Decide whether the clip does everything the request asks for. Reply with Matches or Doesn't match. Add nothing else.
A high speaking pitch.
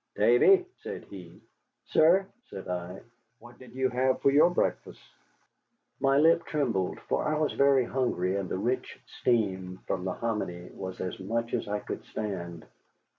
Doesn't match